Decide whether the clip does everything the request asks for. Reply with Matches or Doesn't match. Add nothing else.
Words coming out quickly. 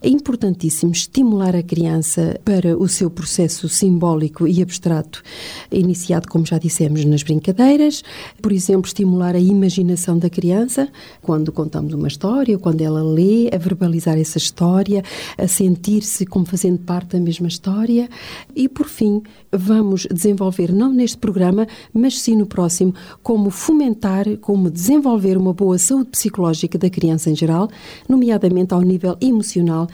Doesn't match